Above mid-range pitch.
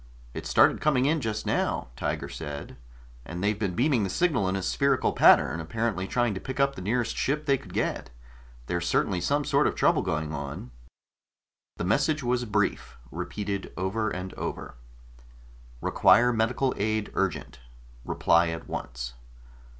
No: low, 105 Hz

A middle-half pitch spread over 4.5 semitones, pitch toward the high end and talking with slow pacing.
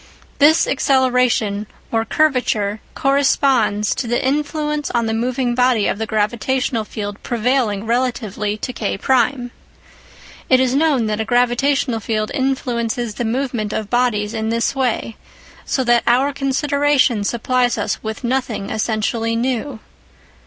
No: average, 3.2 semitones; high, 240 Hz; slow, 130 wpm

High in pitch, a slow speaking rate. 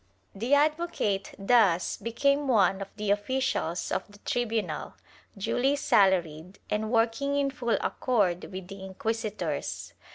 Yes: high, 210 Hz; slow, 130 wpm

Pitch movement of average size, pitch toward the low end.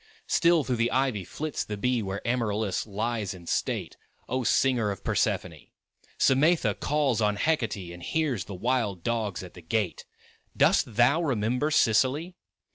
Yes: average, 4.6 semitones; low, 115 Hz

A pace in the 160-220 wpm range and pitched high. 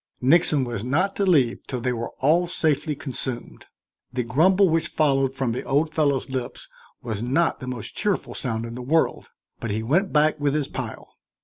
No: average, 190 wpm; low, 135 Hz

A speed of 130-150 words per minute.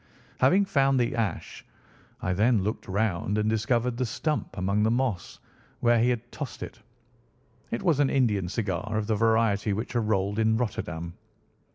No: average, 170 wpm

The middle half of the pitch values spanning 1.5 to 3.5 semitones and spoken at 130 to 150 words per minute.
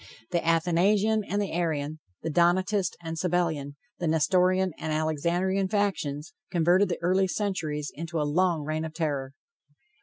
Yes: average, 3.1 semitones; average, 145 wpm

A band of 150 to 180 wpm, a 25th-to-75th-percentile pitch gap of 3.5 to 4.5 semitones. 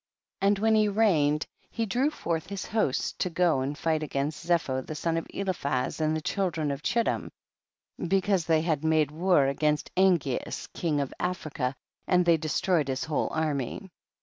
Yes: average, 175 wpm; average, 4.2 semitones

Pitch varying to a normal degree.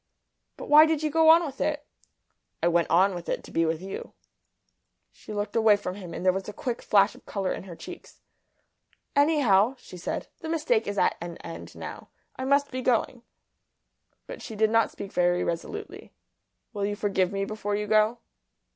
No: wide, 6.0 semitones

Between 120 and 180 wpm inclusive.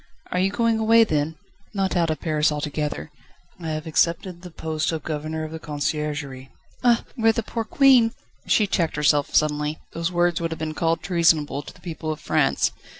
No: average, 195 wpm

